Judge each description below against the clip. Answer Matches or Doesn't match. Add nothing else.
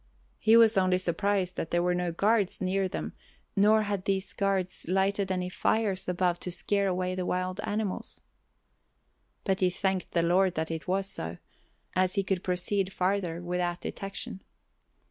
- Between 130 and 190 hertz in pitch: Matches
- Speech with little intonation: Matches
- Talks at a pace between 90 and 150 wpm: Doesn't match